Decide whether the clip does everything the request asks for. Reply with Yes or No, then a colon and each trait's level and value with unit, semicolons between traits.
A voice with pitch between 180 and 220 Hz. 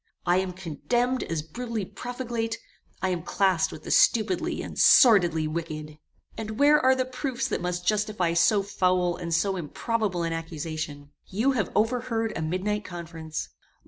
Yes: medium, 185 Hz